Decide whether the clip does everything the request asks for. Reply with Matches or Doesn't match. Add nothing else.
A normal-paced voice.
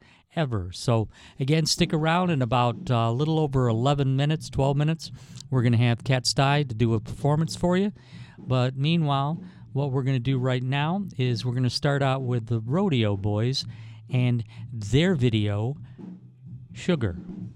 Matches